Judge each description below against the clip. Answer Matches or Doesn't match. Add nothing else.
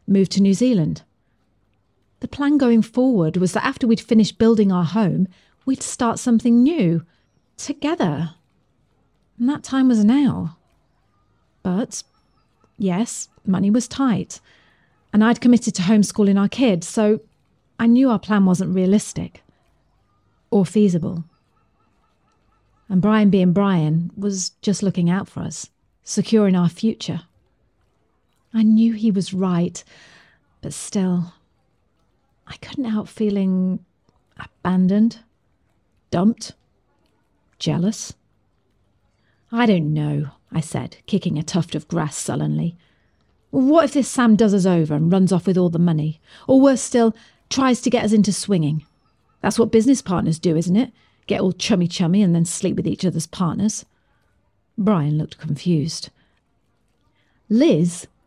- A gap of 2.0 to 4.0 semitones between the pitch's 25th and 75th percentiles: Doesn't match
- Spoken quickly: Doesn't match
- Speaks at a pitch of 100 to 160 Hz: Doesn't match